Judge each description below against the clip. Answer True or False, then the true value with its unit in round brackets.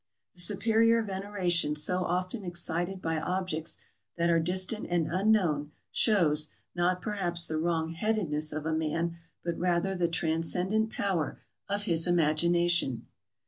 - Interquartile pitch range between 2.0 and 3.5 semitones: True (2.8 semitones)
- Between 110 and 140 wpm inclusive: True (135 wpm)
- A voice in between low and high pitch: True (175 Hz)